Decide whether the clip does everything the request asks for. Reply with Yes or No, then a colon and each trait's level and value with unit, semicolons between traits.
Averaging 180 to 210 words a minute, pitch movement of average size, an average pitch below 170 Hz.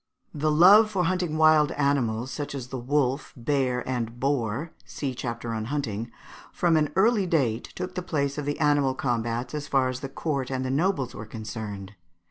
Yes: average, 185 wpm; average, 4.2 semitones; medium, 140 Hz